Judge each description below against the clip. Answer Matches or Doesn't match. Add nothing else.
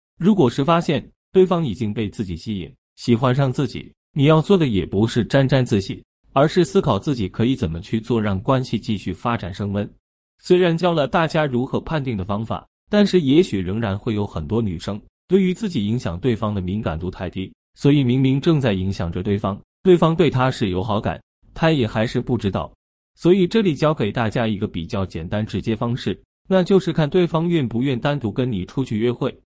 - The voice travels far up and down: Matches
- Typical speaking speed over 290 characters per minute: Matches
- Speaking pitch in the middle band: Doesn't match